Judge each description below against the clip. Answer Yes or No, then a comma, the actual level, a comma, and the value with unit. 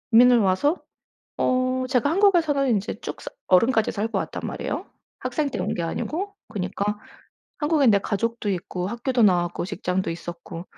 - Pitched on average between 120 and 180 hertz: No, high, 225 Hz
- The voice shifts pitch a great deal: Yes, wide, 6.0 semitones